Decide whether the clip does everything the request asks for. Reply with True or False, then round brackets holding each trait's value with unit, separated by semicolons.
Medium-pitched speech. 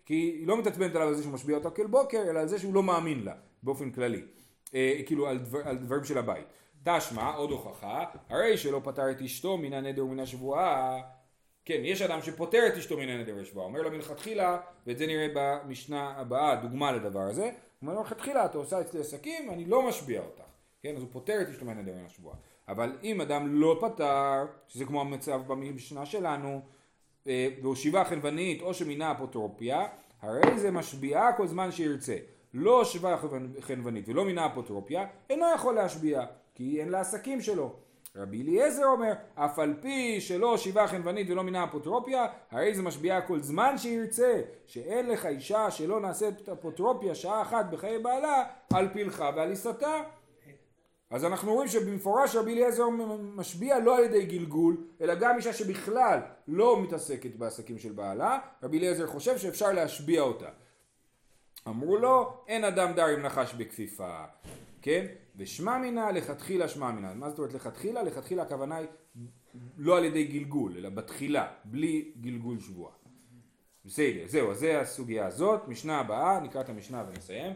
True (160 Hz)